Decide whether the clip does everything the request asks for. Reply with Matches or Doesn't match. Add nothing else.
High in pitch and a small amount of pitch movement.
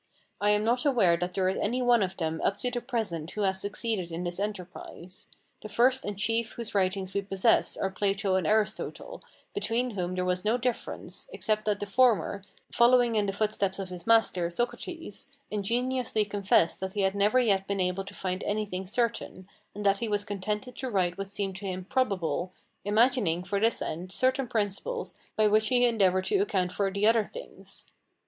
Doesn't match